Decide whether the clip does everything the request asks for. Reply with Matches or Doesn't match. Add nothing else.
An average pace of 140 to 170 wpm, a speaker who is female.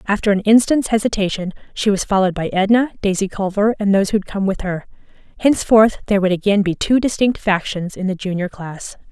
Doesn't match